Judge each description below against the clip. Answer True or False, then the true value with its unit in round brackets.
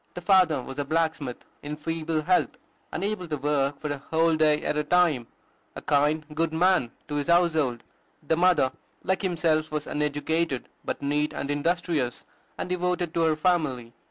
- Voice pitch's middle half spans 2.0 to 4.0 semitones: True (2.8 semitones)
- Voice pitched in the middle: True (155 Hz)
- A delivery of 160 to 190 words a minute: True (170 wpm)